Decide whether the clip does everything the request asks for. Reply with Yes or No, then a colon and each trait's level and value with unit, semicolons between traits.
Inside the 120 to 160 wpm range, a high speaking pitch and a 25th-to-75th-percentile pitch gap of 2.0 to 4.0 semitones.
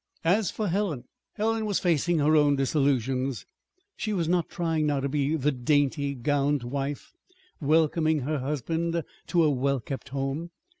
No: average, 155 wpm; medium, 150 Hz; average, 3.3 semitones